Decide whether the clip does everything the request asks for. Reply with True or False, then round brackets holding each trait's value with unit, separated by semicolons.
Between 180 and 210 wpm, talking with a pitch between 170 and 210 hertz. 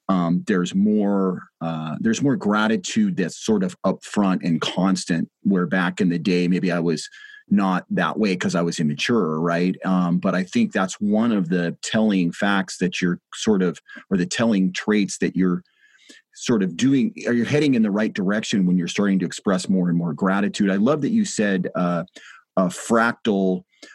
False (190 wpm; 95 Hz)